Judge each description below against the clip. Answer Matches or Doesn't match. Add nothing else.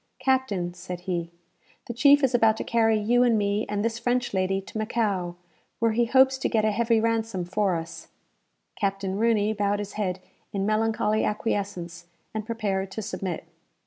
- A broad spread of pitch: Doesn't match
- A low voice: Doesn't match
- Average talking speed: Matches